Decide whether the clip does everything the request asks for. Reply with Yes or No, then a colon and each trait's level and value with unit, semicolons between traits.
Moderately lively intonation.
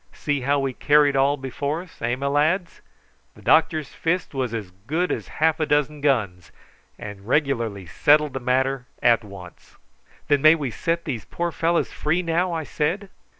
Yes: average, 4.2 semitones